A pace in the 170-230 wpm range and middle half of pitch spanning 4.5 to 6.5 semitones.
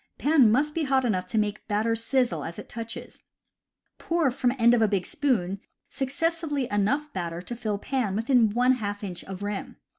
Yes: average, 185 wpm; average, 4.8 semitones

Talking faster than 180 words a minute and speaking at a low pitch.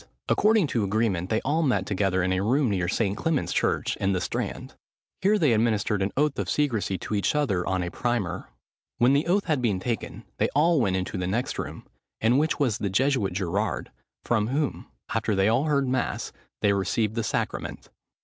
Yes: average, 195 wpm; low, 110 Hz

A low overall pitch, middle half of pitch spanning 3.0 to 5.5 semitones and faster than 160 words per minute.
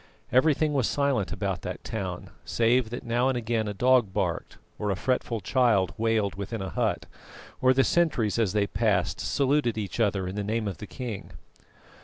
Yes: low, 110 Hz; average, 4.0 semitones; average, 185 wpm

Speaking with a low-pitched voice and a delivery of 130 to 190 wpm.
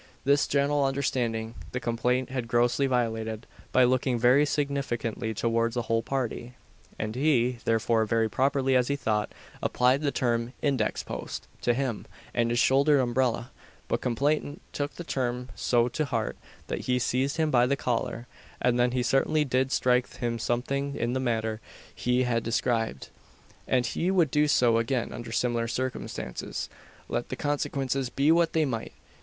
Yes: low, 125 Hz; average, 165 wpm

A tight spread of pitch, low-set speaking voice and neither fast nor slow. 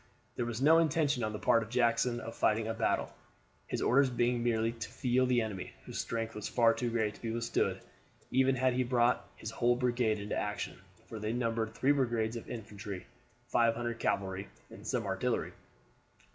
Yes: narrow, 1.9 semitones; low, 115 Hz; average, 185 wpm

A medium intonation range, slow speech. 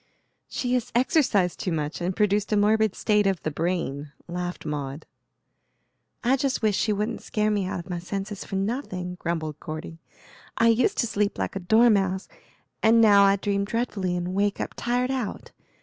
No: average, 3.7 semitones; average, 180 wpm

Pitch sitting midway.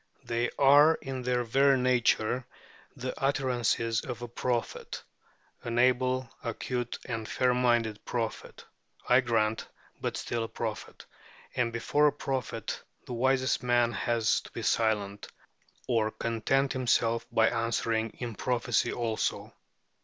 No: low, 120 Hz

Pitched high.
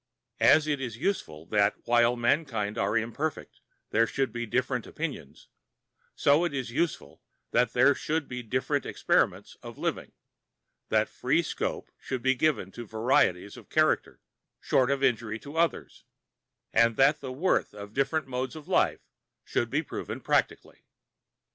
No: low, 130 Hz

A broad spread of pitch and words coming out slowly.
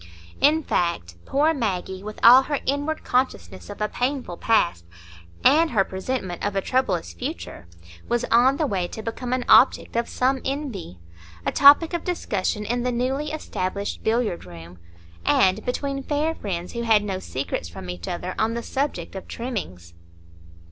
No: wide, 6.5 semitones; average, 160 wpm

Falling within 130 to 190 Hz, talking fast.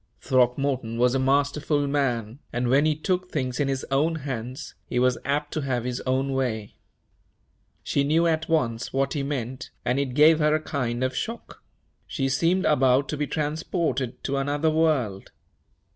No: low, 135 Hz; average, 175 wpm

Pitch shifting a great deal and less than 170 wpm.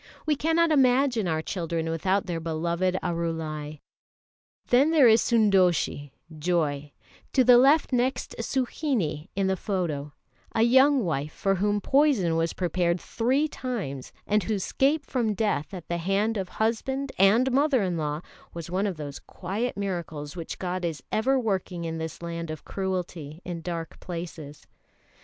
Yes: wide, 6.6 semitones; average, 155 wpm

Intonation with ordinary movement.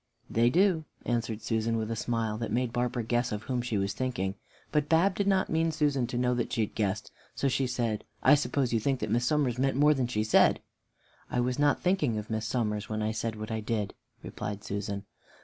Yes: average, 3.8 semitones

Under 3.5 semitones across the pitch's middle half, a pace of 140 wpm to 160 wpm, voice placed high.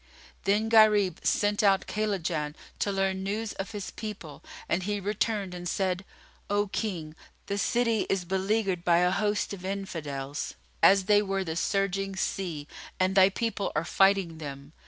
Yes: narrow, 2.5 semitones; average, 155 wpm; high, 195 Hz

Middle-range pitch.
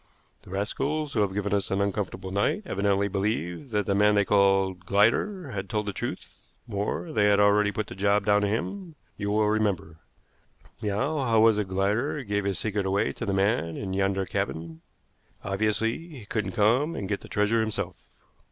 No: low, 105 Hz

